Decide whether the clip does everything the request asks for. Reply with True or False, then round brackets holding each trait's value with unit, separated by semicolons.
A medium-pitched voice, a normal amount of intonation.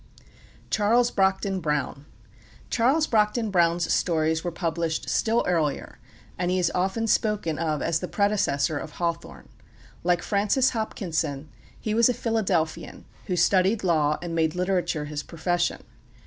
True (175 Hz; 4.5 semitones)